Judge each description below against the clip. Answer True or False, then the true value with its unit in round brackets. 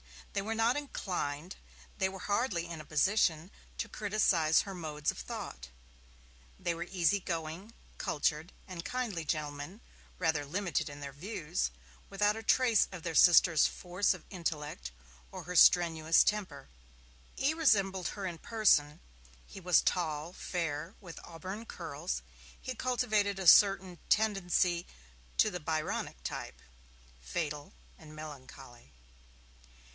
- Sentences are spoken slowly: True (130 wpm)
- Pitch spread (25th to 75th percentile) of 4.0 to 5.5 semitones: True (4.6 semitones)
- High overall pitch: False (175 Hz)